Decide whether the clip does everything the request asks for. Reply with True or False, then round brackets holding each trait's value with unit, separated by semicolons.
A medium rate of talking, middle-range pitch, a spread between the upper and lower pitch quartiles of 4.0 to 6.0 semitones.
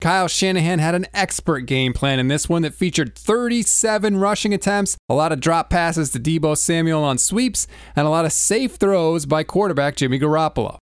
True (195 wpm; 165 Hz; 4.3 semitones)